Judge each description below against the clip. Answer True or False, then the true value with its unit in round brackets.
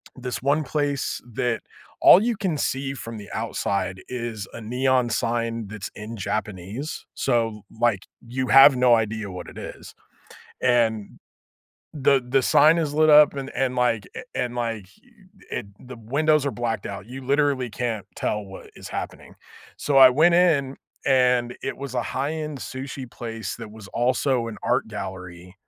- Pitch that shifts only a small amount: False (3.7 semitones)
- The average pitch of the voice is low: True (125 Hz)